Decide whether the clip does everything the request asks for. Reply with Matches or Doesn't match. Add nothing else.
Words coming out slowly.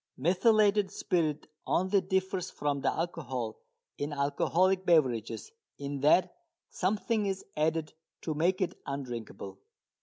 Matches